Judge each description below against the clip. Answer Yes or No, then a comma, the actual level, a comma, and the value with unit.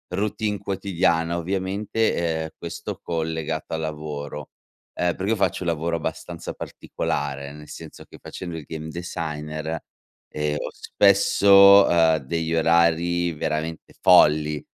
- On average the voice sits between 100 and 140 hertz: No, very low, 80 Hz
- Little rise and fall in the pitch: No, average, 3.1 semitones